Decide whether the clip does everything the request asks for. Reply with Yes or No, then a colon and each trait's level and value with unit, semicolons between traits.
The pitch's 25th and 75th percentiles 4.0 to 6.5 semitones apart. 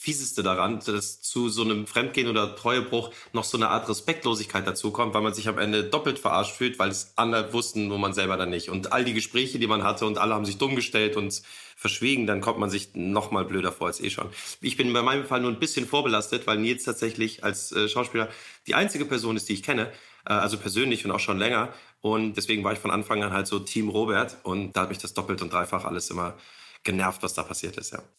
No: average, 3.2 semitones